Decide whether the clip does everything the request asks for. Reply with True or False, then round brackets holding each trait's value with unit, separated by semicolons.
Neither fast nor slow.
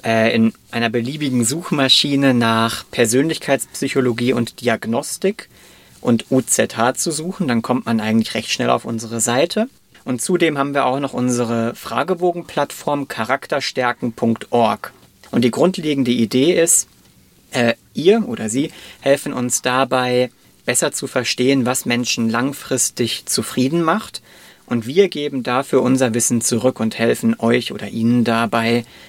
False (130 wpm)